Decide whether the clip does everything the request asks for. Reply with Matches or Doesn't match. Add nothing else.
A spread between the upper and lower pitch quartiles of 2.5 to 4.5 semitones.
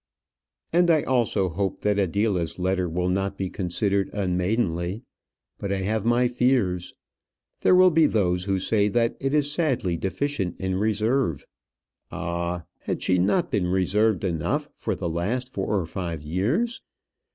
Doesn't match